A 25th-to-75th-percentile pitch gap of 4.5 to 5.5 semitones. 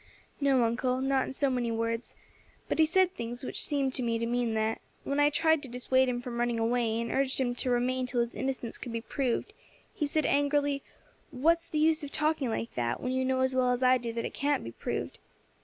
No: average, 3.0 semitones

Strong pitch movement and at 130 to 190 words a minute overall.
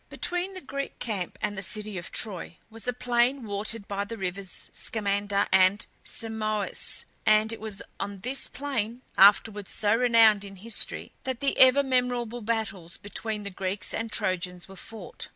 No: average, 3.1 semitones; average, 165 wpm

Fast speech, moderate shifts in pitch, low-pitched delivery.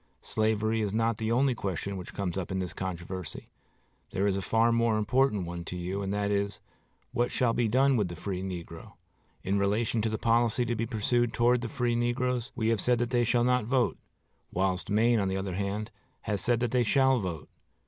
Yes: fast, 215 wpm; average, 3.7 semitones; low, 110 Hz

